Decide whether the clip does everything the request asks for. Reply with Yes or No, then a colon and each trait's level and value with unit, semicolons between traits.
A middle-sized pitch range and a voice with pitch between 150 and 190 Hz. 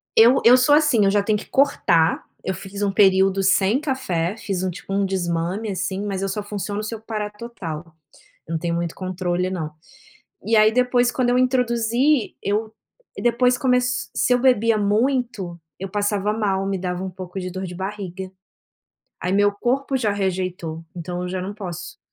No: average, 4.0 semitones; high, 200 Hz